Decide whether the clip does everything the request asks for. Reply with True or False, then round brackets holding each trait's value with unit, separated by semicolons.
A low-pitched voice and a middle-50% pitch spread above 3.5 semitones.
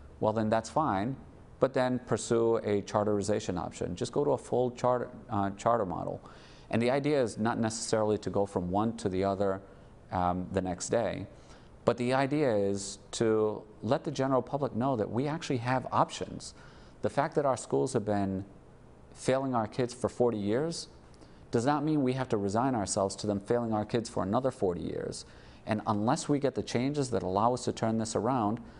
True (110 Hz; 4.0 semitones)